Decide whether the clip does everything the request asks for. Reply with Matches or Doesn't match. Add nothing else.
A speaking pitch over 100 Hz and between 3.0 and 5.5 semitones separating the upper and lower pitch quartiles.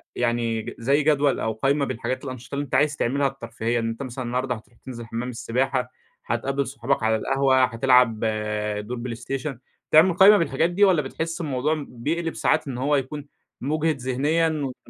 Matches